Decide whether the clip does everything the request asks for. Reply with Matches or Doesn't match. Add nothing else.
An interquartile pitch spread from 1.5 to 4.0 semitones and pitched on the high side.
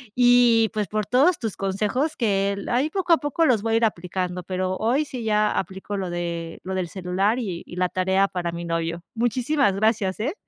Doesn't match